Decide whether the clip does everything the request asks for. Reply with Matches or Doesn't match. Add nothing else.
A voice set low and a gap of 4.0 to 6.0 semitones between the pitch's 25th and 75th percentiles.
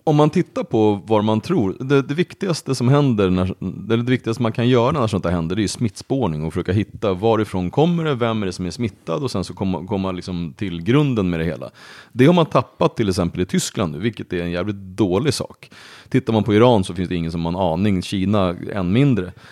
Matches